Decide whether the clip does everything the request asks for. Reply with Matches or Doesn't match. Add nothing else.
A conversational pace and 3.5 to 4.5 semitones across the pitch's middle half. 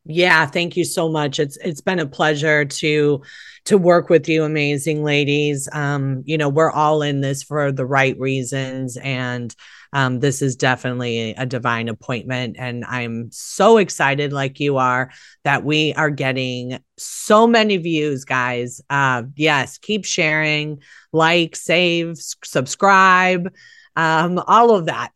Matches